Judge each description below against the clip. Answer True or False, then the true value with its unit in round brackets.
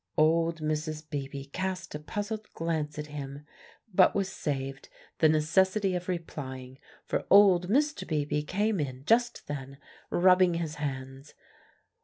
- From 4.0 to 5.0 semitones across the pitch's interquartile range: True (4.5 semitones)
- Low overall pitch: False (155 Hz)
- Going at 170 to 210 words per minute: False (135 wpm)